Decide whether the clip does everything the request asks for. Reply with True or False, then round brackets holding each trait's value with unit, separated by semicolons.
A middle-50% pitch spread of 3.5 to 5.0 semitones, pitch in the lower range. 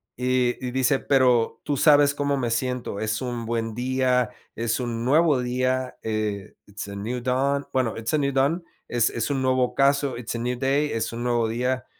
False (2.4 semitones; 125 Hz)